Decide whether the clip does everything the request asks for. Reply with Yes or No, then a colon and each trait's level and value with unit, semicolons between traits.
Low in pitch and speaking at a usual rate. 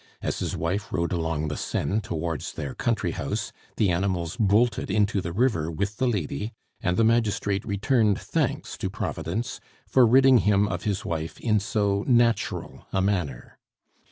Yes: low, 100 Hz; average, 160 wpm